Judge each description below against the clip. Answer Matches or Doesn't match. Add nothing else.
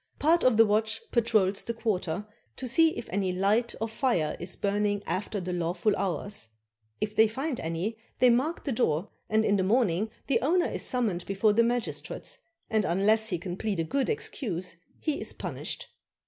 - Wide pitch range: Doesn't match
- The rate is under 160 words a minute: Doesn't match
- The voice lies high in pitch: Matches